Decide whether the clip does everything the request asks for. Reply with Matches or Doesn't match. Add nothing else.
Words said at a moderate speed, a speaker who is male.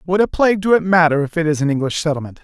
Doesn't match